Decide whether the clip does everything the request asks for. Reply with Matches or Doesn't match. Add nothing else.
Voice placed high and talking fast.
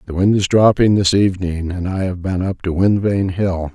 Doesn't match